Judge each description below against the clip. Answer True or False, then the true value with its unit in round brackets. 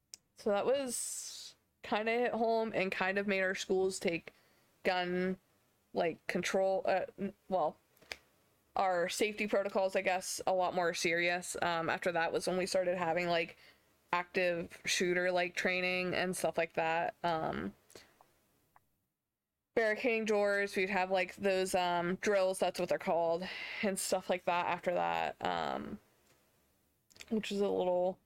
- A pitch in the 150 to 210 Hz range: True (185 Hz)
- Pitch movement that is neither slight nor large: False (1.9 semitones)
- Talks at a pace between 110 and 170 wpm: True (145 wpm)